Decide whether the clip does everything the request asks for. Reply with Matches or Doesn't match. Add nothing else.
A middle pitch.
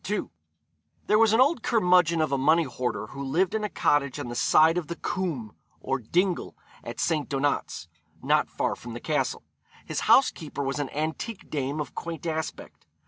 Matches